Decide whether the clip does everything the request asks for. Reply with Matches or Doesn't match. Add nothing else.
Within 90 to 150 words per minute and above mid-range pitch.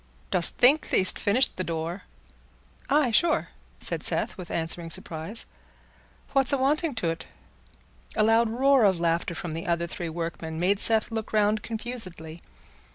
Matches